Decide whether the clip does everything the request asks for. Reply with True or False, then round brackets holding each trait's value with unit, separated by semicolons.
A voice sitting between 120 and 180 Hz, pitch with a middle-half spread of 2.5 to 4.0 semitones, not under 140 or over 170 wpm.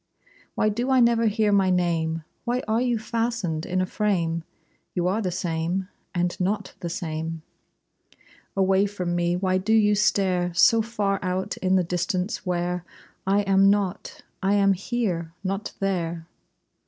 False (190 Hz; 2.9 semitones; 155 wpm)